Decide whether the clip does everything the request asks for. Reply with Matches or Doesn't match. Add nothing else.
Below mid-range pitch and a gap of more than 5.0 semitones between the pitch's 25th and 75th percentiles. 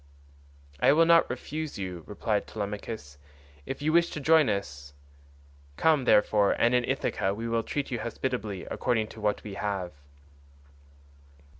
Matches